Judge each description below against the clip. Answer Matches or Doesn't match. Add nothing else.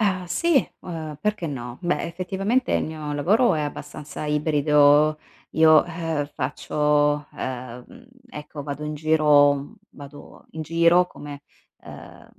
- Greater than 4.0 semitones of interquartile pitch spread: Doesn't match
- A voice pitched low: Doesn't match